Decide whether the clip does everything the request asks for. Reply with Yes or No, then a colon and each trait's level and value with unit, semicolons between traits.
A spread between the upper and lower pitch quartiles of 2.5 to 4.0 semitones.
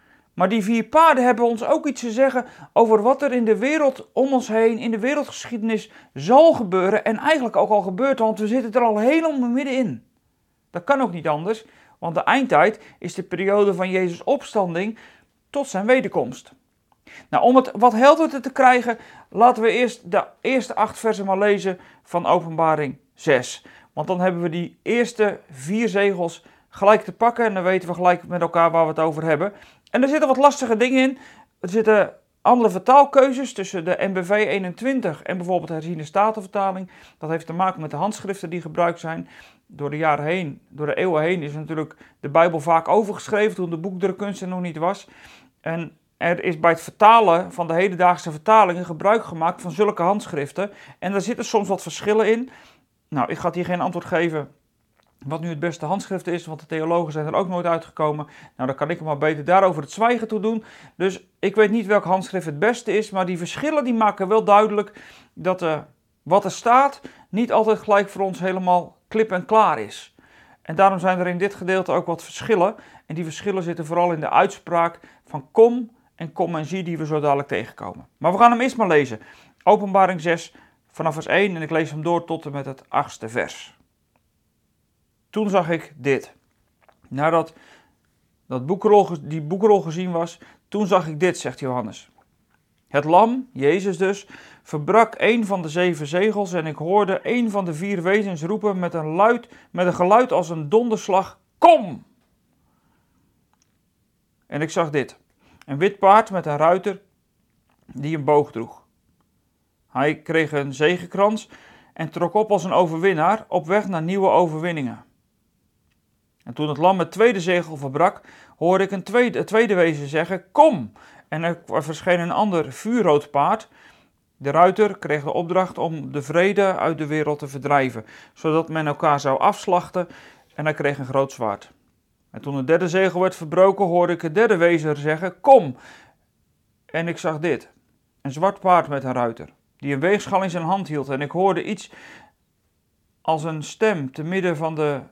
No: average, 5.0 semitones